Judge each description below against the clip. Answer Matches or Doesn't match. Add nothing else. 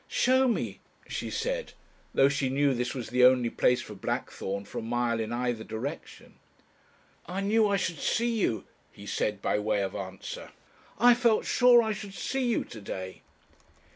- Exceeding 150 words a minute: Matches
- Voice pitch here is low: Matches